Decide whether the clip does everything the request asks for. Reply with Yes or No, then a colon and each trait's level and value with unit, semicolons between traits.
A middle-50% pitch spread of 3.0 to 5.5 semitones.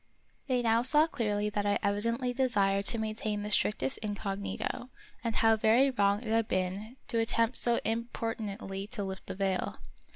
No: narrow, 2.5 semitones